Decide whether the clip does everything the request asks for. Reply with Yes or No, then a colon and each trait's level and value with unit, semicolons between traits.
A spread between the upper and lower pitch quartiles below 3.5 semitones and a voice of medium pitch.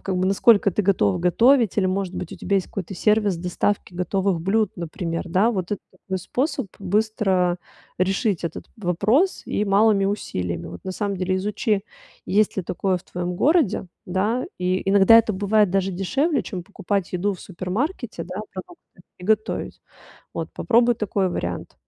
No: average, 2.8 semitones; high, 195 Hz